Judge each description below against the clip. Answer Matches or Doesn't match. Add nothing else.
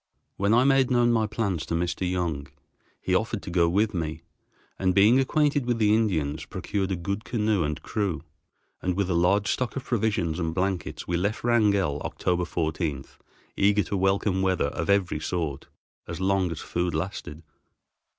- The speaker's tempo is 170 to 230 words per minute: Matches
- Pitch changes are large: Doesn't match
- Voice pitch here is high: Doesn't match